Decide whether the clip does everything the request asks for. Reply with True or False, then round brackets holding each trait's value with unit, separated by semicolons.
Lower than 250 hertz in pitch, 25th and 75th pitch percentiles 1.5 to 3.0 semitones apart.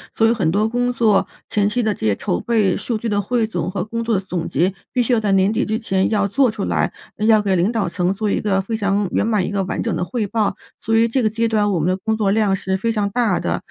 True (210 Hz; 2.7 semitones)